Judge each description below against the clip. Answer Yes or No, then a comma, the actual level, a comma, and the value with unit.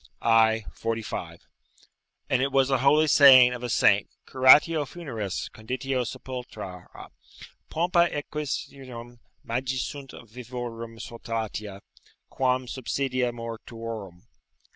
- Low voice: Yes, low, 125 Hz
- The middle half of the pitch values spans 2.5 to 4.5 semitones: Yes, average, 2.9 semitones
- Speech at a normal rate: No, slow, 100 wpm